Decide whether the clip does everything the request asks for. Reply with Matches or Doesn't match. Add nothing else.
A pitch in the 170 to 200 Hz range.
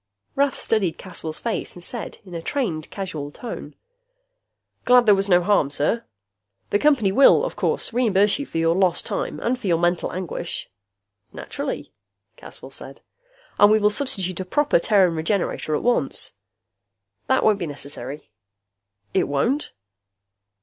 Matches